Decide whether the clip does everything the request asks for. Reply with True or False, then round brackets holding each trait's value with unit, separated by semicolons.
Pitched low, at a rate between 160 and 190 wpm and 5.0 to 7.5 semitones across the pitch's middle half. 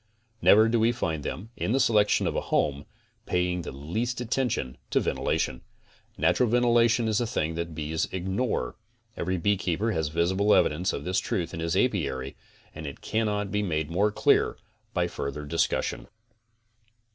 True (95 Hz; 165 wpm; 5.5 semitones)